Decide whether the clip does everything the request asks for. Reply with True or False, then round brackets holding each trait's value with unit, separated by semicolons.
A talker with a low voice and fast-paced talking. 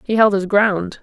False (200 Hz; 235 wpm)